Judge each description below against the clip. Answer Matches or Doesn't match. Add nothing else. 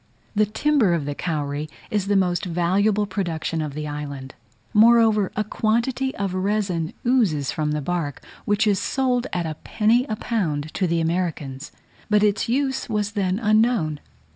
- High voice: Matches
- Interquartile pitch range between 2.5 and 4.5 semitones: Doesn't match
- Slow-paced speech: Doesn't match